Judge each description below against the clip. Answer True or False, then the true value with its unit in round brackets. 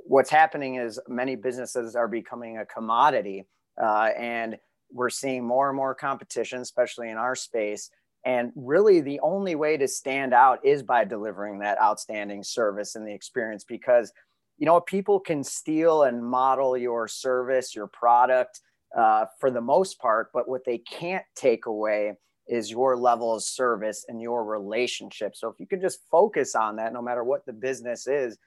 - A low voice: True (120 Hz)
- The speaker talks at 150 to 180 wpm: True (175 wpm)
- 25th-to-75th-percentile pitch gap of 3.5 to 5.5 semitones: False (3.1 semitones)